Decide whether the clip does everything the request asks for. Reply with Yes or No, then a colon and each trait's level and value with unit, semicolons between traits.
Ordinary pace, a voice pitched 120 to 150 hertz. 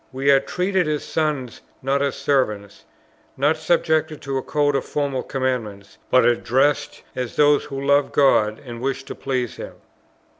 Yes: average, 160 wpm; low, 135 Hz